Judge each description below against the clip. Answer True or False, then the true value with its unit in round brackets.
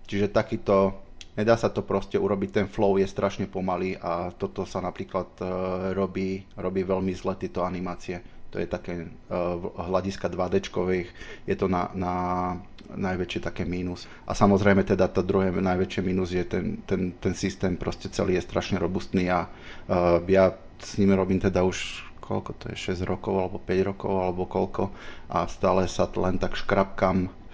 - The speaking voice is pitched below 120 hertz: True (95 Hz)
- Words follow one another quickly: True (170 wpm)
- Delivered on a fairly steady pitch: True (1.4 semitones)